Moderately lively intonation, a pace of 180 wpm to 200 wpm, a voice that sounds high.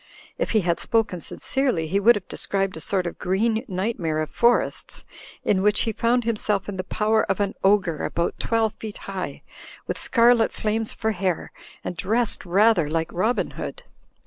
Yes: average, 3.6 semitones; average, 195 wpm; high, 205 Hz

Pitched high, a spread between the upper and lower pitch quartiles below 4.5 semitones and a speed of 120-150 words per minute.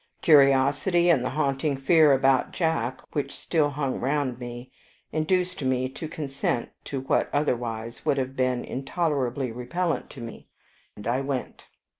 No: low, 135 Hz; average, 2.9 semitones; average, 145 wpm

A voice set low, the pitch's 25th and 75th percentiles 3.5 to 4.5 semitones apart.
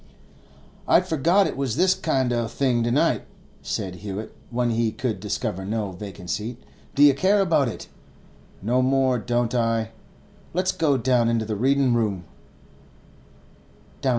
Yes: low, 120 Hz; average, 3.8 semitones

